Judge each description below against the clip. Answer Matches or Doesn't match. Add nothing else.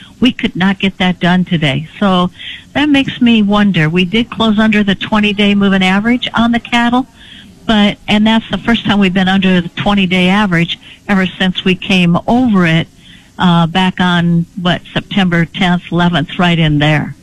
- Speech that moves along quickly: Doesn't match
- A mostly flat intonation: Doesn't match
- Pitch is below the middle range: Doesn't match